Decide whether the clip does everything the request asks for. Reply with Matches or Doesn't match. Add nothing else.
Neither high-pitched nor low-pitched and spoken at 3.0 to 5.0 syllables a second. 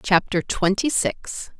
Doesn't match